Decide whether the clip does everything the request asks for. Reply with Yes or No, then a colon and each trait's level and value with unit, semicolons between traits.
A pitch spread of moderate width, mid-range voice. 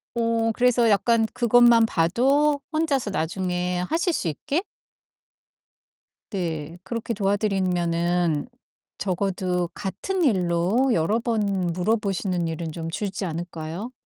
No: average, 5.0 semitones; high, 195 Hz